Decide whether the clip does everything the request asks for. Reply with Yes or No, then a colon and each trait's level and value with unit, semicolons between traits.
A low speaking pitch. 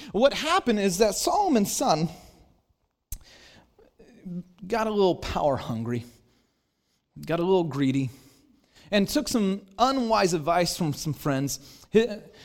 No: high, 190 Hz